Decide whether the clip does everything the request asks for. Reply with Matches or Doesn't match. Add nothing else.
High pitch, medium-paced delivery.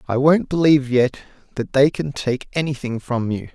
Doesn't match